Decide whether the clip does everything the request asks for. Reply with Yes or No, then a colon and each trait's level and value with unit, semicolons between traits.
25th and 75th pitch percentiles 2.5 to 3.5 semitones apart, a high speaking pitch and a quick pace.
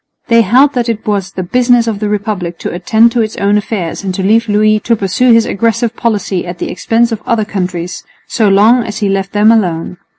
Yes: average, 3.0 semitones; high, 210 Hz; fast, 225 wpm